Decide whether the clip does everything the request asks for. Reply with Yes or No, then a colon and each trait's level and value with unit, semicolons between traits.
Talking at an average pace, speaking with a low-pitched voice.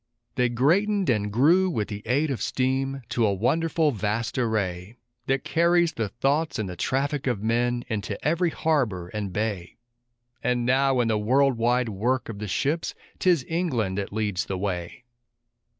Yes: average, 165 wpm; low, 120 Hz